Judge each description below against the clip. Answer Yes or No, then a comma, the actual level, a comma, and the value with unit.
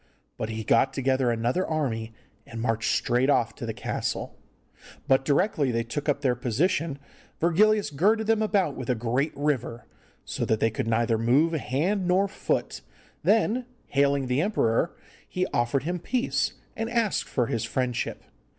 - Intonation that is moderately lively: No, wide, 7.1 semitones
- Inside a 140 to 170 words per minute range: Yes, average, 160 wpm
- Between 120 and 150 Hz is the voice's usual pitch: Yes, medium, 140 Hz